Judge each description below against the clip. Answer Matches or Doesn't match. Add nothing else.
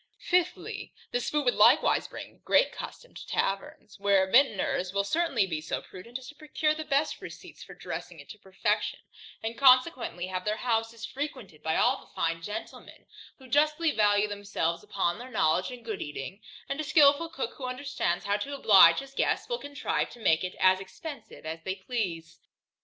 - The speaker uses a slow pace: Doesn't match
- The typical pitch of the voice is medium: Doesn't match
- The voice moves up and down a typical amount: Doesn't match